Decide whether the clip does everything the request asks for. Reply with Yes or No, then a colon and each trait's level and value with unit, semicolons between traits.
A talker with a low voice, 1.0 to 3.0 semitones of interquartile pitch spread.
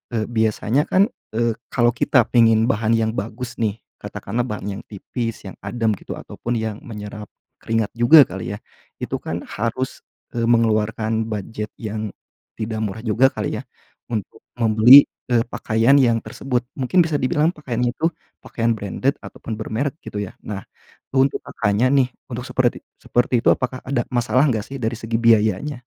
Yes: low, 115 Hz; narrow, 2.5 semitones